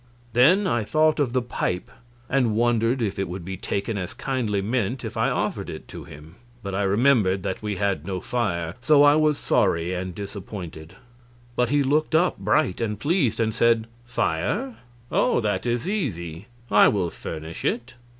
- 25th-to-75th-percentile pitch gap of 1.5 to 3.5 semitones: No, average, 5.2 semitones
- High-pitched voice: No, low, 110 Hz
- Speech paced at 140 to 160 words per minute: No, average, 180 wpm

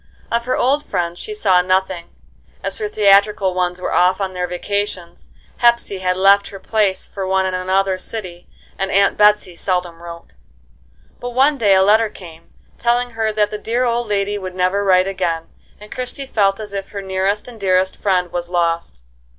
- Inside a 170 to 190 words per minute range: Yes, average, 185 wpm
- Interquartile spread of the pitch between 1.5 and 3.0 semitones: Yes, narrow, 2.5 semitones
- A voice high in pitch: Yes, high, 195 Hz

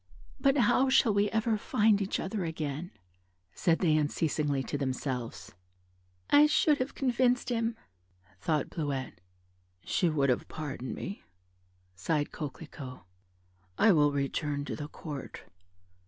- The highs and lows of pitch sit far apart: Yes, wide, 7.6 semitones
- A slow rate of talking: Yes, slow, 125 wpm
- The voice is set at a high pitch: No, medium, 160 Hz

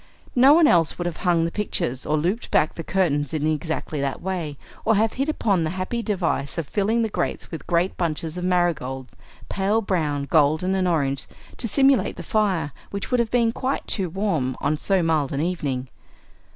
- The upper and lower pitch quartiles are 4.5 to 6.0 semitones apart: Yes, average, 5.2 semitones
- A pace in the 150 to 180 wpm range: No, average, 200 wpm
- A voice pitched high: No, medium, 175 Hz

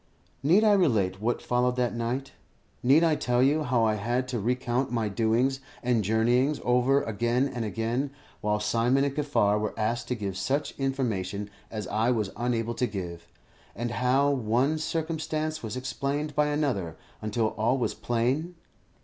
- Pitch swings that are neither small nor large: Yes, average, 3.8 semitones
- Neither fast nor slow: Yes, average, 160 wpm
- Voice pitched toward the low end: Yes, low, 120 Hz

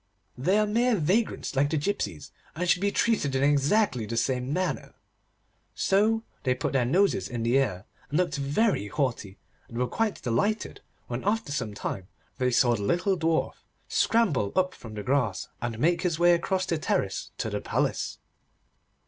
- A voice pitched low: No, medium, 145 Hz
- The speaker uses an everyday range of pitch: No, wide, 7.9 semitones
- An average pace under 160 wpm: No, average, 175 wpm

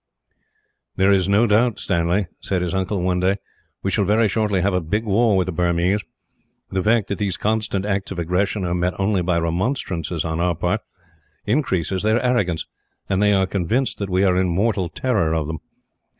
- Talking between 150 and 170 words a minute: No, average, 195 wpm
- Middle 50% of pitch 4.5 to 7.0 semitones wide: No, average, 2.8 semitones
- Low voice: Yes, very low, 95 Hz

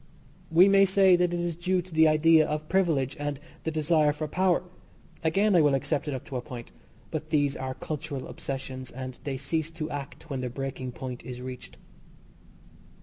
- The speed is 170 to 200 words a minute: Yes, average, 195 wpm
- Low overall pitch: No, medium, 150 Hz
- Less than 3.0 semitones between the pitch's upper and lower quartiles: No, average, 3.8 semitones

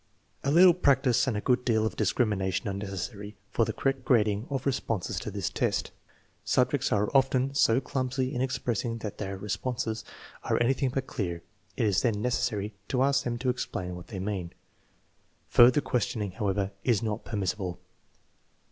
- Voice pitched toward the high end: No, low, 115 Hz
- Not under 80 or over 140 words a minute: No, average, 170 wpm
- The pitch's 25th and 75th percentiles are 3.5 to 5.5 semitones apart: Yes, average, 4.1 semitones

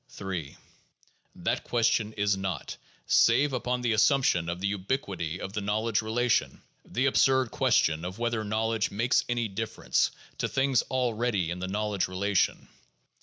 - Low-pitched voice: Yes, low, 110 Hz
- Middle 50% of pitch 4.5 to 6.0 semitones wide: No, average, 4.0 semitones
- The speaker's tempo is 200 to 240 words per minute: No, average, 145 wpm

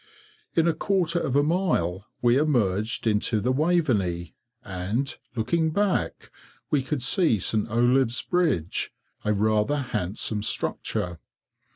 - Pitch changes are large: Yes, wide, 6.9 semitones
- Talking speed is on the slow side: Yes, slow, 125 wpm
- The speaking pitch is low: Yes, low, 120 Hz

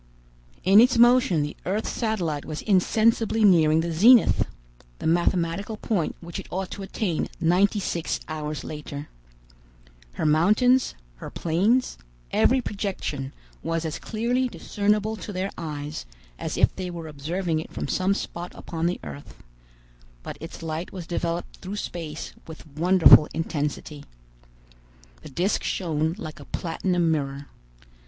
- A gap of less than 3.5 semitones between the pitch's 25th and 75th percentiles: No, average, 4.4 semitones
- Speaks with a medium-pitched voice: Yes, medium, 175 Hz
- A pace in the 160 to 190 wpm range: No, average, 140 wpm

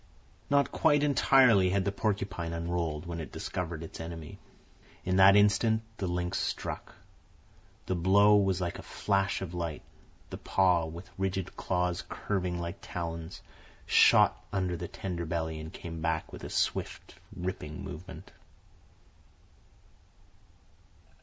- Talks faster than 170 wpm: No, slow, 135 wpm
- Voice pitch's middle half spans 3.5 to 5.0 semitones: No, narrow, 2.6 semitones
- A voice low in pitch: Yes, very low, 90 Hz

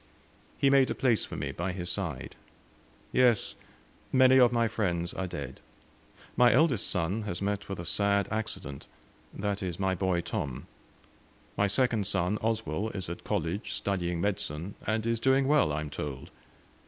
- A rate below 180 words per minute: Yes, average, 165 wpm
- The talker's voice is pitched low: Yes, low, 100 Hz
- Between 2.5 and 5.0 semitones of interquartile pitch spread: Yes, average, 4.6 semitones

